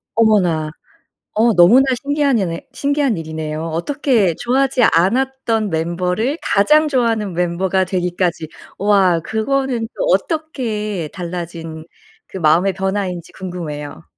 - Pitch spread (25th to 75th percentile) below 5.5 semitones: No, wide, 6.1 semitones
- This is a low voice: No, high, 190 Hz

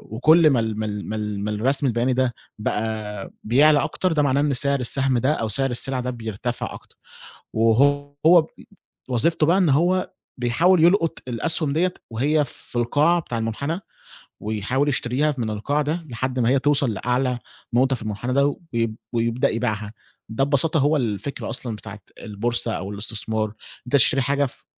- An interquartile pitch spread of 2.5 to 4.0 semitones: No, average, 4.4 semitones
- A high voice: No, low, 125 Hz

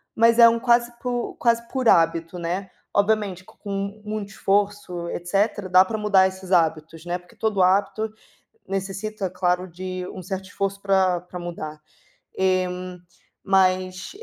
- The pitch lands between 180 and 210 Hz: Yes, high, 190 Hz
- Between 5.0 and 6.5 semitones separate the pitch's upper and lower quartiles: No, narrow, 2.4 semitones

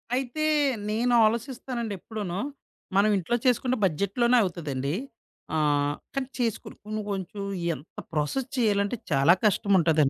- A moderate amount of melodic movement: No, wide, 6.8 semitones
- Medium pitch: No, high, 200 Hz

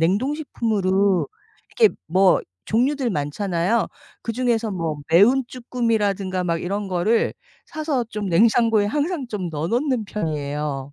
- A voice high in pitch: Yes, high, 205 Hz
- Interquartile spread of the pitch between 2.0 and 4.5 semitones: No, wide, 5.4 semitones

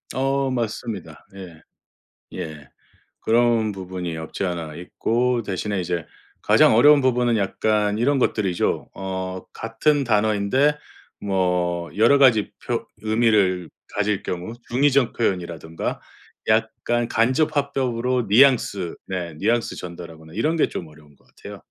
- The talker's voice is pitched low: Yes, low, 105 Hz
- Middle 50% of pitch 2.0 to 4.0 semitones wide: No, average, 5.2 semitones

